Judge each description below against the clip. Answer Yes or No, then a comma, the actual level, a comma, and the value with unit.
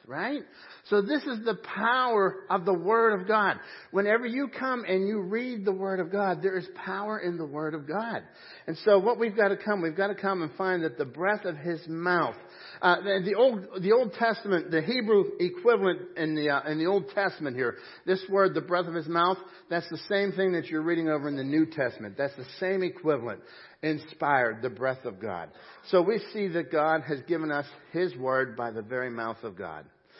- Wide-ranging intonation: No, average, 4.5 semitones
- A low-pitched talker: No, medium, 185 Hz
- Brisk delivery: Yes, fast, 220 wpm